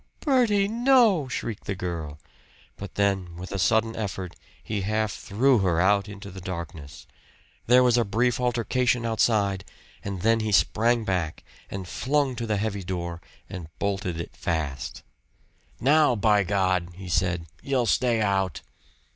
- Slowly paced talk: No, average, 150 wpm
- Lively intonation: No, average, 4.4 semitones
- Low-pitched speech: Yes, low, 100 Hz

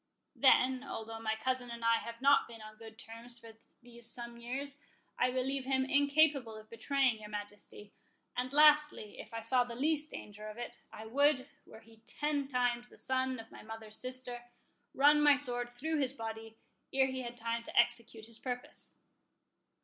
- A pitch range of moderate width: Yes, average, 3.0 semitones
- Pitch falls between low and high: No, high, 245 Hz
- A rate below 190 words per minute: Yes, average, 180 wpm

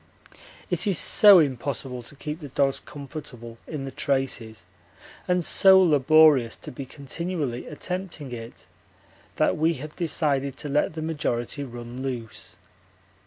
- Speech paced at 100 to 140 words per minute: Yes, slow, 135 wpm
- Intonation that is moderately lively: Yes, average, 3.9 semitones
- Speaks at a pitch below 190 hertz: Yes, medium, 140 Hz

